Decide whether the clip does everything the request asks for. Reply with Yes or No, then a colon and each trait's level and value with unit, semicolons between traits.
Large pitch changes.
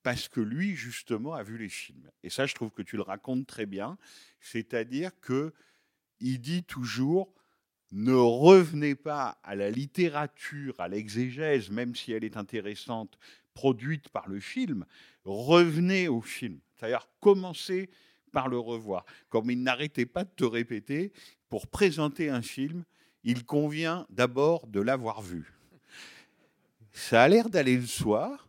Yes: wide, 6.1 semitones